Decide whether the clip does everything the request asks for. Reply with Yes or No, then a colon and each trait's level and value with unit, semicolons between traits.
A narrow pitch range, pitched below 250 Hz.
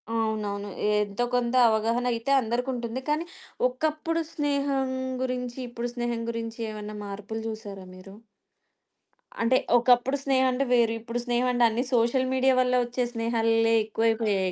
Yes: narrow, 2.3 semitones; high, 235 Hz